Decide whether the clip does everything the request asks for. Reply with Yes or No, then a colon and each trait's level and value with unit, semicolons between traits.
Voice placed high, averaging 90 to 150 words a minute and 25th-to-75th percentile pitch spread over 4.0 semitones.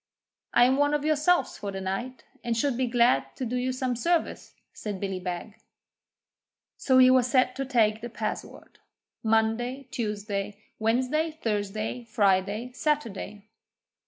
No: high, 235 Hz; average, 145 wpm; average, 3.6 semitones